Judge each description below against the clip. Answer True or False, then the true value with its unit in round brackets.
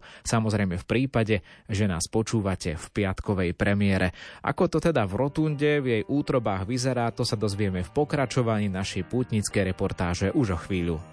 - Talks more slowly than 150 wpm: False (155 wpm)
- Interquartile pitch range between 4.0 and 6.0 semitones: True (4.8 semitones)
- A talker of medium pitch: False (105 Hz)